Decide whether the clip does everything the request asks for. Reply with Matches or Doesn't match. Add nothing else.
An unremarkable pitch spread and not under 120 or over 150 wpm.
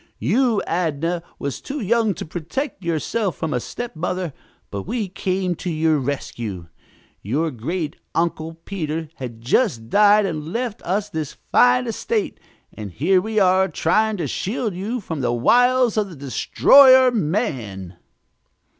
Doesn't match